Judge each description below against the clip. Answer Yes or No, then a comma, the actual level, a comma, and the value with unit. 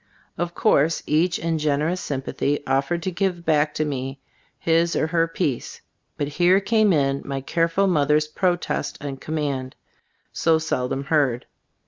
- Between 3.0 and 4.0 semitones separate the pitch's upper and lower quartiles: Yes, average, 3.3 semitones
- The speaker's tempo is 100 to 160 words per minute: Yes, average, 150 wpm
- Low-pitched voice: No, medium, 155 Hz